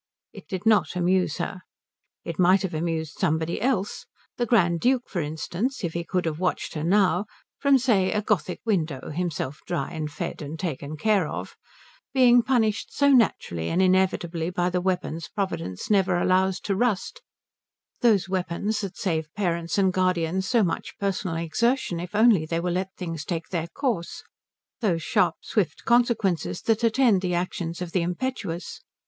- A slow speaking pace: No, average, 165 wpm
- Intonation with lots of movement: No, average, 4.0 semitones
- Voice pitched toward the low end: No, medium, 185 Hz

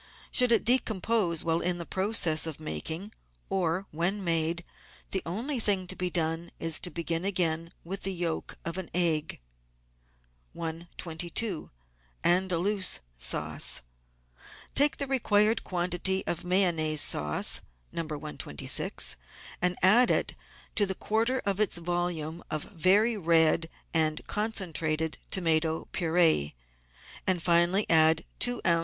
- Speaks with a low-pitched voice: No, medium, 175 Hz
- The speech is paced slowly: Yes, slow, 130 wpm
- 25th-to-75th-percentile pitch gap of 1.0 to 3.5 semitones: Yes, average, 3.0 semitones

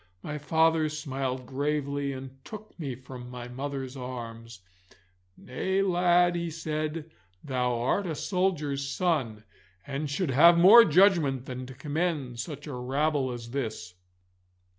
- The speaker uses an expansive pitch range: No, average, 4.2 semitones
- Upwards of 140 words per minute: No, slow, 135 wpm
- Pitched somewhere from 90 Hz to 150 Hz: Yes, medium, 140 Hz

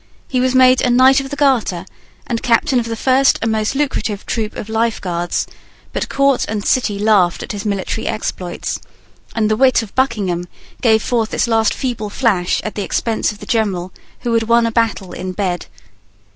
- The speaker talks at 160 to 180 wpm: No, average, 195 wpm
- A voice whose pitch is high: Yes, high, 225 Hz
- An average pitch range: Yes, average, 3.6 semitones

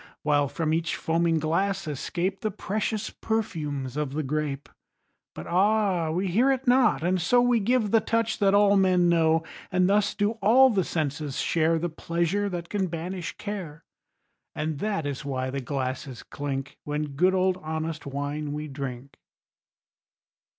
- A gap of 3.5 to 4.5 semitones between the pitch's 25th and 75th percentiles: No, average, 5.1 semitones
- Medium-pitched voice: Yes, medium, 170 Hz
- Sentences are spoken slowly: No, average, 160 wpm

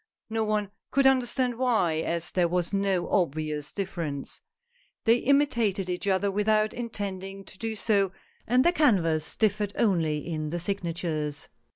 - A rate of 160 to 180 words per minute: No, average, 145 wpm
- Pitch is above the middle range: Yes, high, 195 Hz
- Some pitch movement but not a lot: Yes, average, 4.6 semitones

